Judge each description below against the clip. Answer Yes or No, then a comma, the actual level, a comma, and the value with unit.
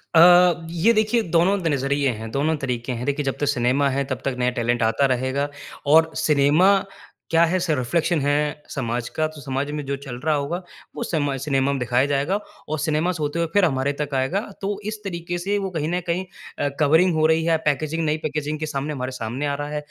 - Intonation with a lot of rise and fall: No, average, 3.4 semitones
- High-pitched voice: No, medium, 150 Hz